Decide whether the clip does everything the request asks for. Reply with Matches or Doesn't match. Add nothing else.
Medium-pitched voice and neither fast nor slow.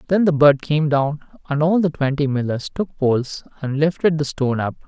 Doesn't match